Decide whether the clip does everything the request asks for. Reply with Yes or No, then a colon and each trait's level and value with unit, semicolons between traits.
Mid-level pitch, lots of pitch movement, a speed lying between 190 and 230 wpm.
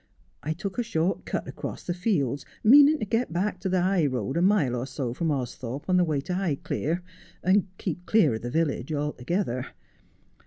Yes: medium, 165 Hz; wide, 5.8 semitones; average, 195 wpm